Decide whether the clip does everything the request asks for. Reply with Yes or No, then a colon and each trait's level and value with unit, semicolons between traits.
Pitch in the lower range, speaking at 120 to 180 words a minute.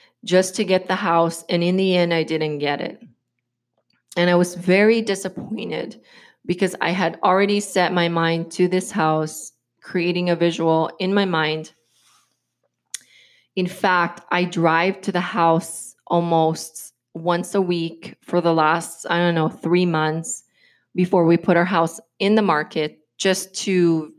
No: medium, 175 Hz; average, 155 wpm